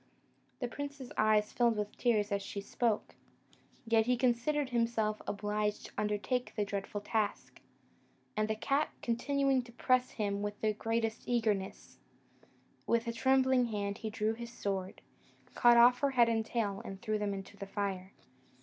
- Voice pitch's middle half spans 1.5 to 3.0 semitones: Yes, average, 2.7 semitones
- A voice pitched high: Yes, high, 220 Hz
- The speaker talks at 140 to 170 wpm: Yes, average, 160 wpm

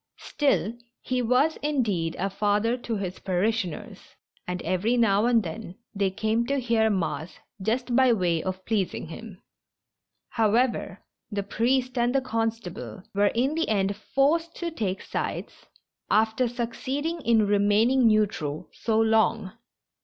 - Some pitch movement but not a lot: Yes, average, 3.9 semitones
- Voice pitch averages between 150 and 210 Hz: No, high, 225 Hz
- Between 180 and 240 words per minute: No, average, 140 wpm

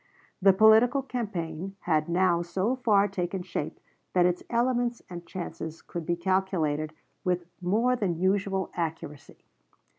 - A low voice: No, medium, 185 Hz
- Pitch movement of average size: Yes, average, 3.3 semitones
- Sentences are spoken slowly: Yes, slow, 130 wpm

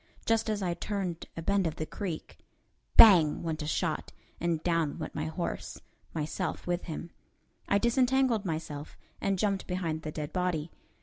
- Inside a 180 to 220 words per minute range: No, average, 165 wpm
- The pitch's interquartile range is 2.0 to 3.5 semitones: No, average, 4.0 semitones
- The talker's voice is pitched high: No, medium, 175 Hz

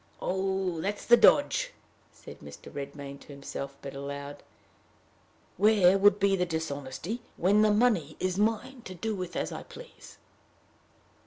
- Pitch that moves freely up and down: Yes, wide, 6.6 semitones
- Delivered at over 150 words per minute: No, average, 145 wpm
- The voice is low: No, medium, 185 Hz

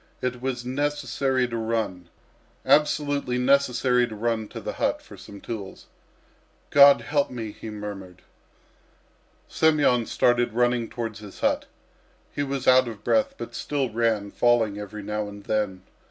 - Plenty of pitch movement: No, average, 3.8 semitones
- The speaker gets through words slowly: No, average, 145 wpm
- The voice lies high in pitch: No, low, 120 Hz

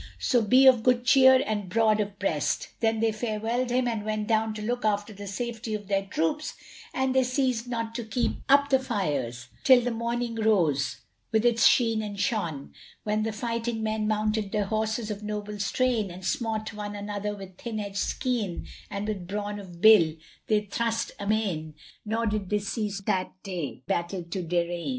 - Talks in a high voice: Yes, high, 215 Hz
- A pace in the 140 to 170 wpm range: No, average, 185 wpm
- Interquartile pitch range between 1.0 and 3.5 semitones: Yes, narrow, 2.6 semitones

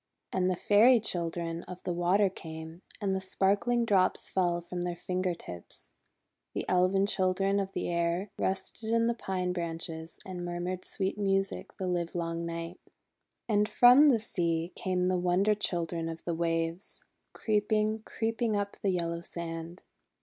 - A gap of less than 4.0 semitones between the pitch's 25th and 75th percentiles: Yes, average, 2.9 semitones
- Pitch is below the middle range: No, medium, 180 Hz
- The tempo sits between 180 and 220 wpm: No, average, 160 wpm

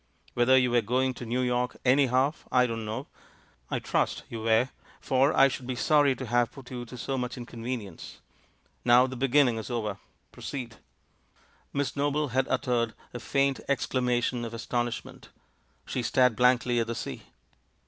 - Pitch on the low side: Yes, low, 125 Hz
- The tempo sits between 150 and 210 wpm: Yes, average, 170 wpm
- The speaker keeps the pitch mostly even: Yes, narrow, 1.8 semitones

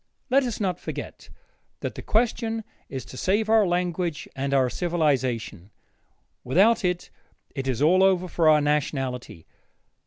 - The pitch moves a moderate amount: No, wide, 6.2 semitones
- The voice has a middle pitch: Yes, medium, 170 Hz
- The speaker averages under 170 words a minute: Yes, average, 145 wpm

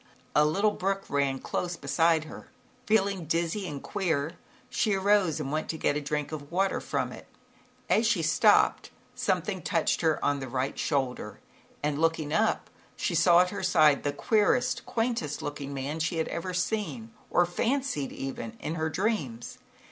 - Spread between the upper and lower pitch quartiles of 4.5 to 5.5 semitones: Yes, average, 5.2 semitones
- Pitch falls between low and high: Yes, medium, 165 Hz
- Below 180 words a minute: Yes, average, 170 wpm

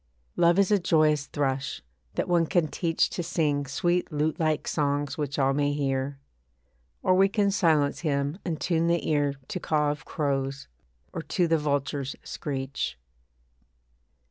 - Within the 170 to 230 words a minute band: No, average, 155 wpm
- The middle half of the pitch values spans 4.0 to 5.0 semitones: No, average, 3.2 semitones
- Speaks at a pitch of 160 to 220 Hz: No, medium, 150 Hz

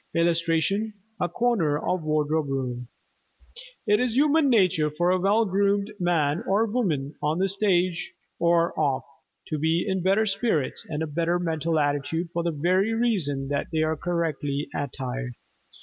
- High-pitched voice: No, medium, 170 Hz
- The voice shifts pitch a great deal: No, average, 4.6 semitones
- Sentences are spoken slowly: No, average, 155 wpm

